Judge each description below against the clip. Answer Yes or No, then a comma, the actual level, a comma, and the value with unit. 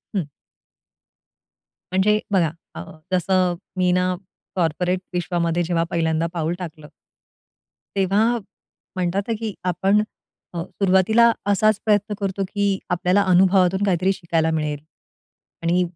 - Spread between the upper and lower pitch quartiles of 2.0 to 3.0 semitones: Yes, narrow, 2.4 semitones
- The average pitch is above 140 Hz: Yes, medium, 185 Hz